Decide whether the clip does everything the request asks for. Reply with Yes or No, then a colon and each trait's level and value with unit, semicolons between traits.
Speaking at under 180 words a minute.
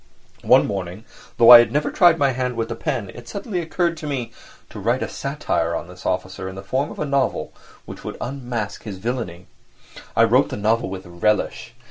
No: fast, 205 wpm